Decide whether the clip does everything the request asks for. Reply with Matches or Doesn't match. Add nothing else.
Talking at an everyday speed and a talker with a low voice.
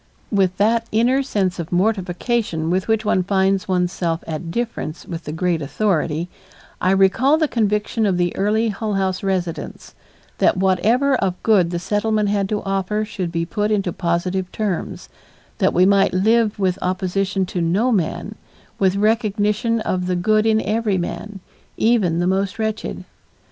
Doesn't match